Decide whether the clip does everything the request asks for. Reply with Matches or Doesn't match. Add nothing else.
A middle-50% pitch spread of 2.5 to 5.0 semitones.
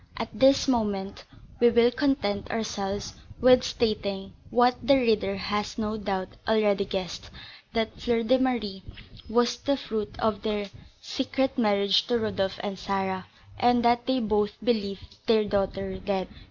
Matches